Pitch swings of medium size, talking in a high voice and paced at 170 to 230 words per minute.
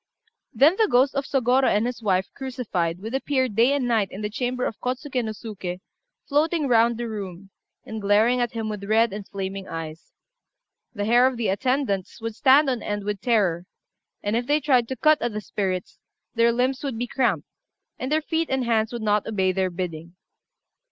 Yes: average, 4.3 semitones; high, 230 Hz; average, 200 wpm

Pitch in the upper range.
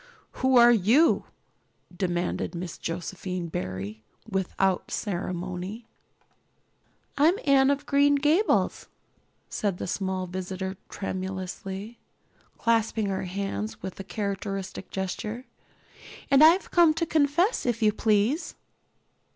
Yes: high, 200 Hz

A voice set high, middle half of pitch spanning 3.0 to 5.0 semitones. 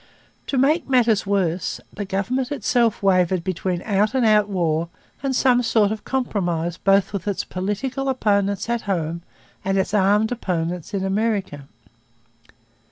Yes: high, 200 Hz; average, 4.0 semitones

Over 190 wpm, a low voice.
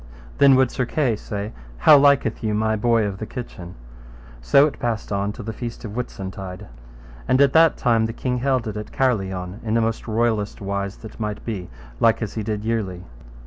Yes: average, 200 wpm; low, 110 Hz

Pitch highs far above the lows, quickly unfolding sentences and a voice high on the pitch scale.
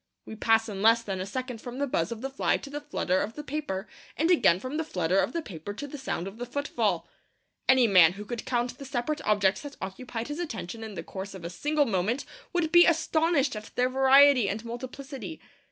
Yes: wide, 5.9 semitones; fast, 230 wpm; high, 245 Hz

